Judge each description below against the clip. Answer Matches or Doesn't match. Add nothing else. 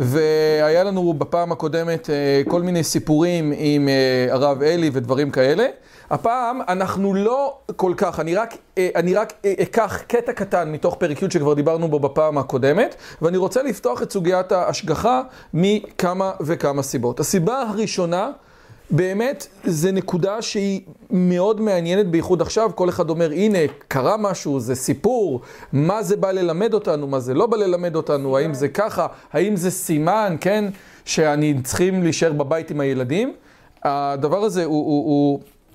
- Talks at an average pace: Matches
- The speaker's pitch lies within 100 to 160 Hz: Doesn't match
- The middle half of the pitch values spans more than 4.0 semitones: Matches